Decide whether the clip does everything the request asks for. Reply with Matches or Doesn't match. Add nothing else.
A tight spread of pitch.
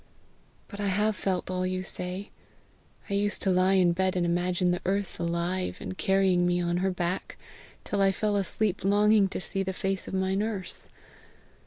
Matches